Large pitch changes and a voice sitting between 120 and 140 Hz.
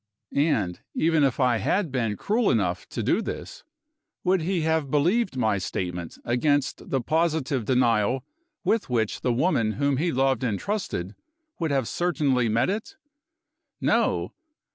Yes: wide, 5.8 semitones; low, 135 Hz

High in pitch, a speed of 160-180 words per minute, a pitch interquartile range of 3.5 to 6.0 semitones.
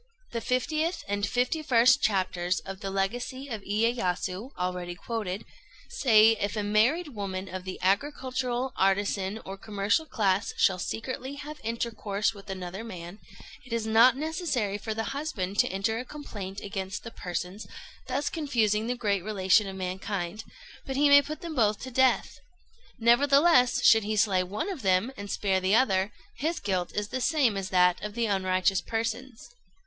Yes: high, 215 Hz; average, 165 wpm; average, 4.7 semitones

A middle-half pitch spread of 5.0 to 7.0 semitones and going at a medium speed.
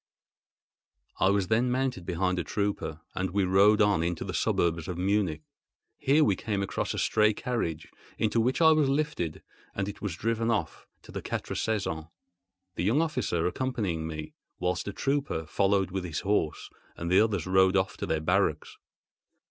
No: average, 4.2 semitones; average, 170 wpm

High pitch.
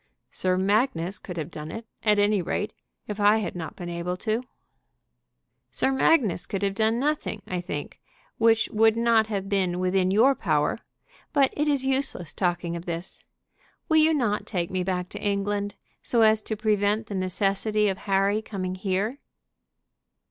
Yes: high, 205 Hz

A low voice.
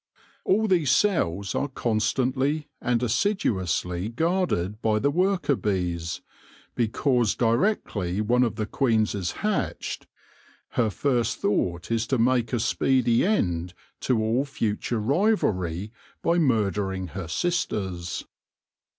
Yes: low, 115 Hz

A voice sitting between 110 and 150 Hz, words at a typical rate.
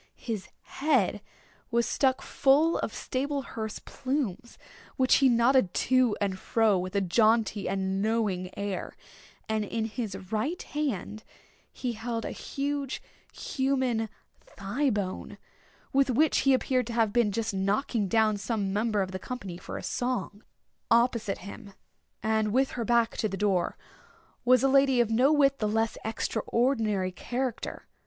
No: high, 225 Hz; average, 150 wpm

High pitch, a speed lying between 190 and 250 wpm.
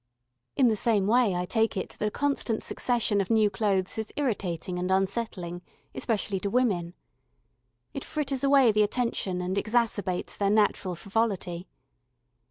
No: high, 210 Hz; average, 150 wpm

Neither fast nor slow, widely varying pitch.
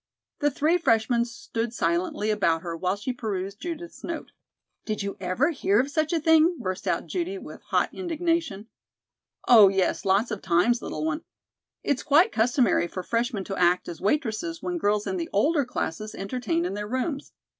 Yes: average, 175 wpm; wide, 8.0 semitones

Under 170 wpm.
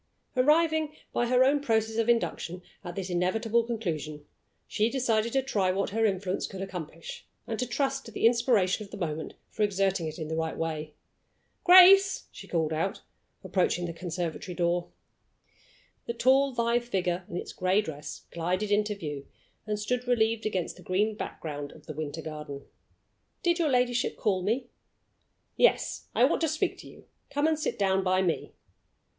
No: average, 175 wpm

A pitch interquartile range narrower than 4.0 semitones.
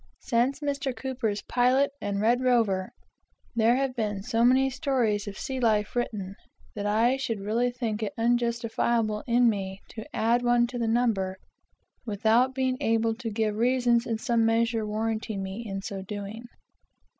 Yes: narrow, 2.6 semitones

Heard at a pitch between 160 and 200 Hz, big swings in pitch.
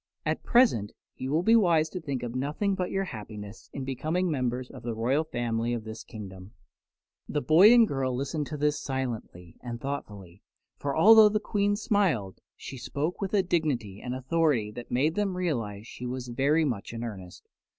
No: low, 135 Hz; wide, 6.2 semitones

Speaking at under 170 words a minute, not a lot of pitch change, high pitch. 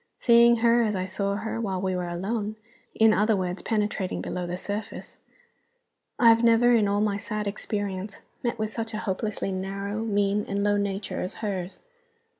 No: average, 180 wpm; narrow, 2.3 semitones; high, 205 Hz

